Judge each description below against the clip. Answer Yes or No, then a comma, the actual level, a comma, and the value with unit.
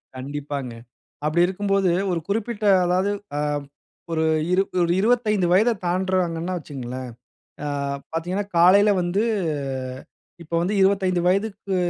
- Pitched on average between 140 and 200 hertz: Yes, medium, 185 Hz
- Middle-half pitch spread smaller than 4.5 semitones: Yes, average, 3.3 semitones